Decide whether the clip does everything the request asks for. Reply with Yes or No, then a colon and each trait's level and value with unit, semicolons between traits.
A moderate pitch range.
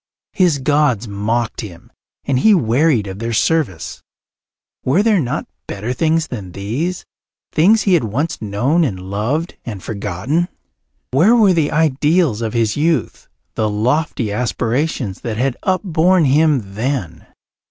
No: wide, 7.1 semitones